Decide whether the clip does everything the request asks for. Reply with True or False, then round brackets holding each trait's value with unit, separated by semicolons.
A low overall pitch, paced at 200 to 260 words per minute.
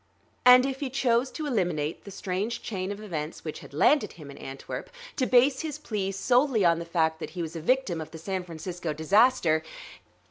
False (190 Hz; 205 wpm)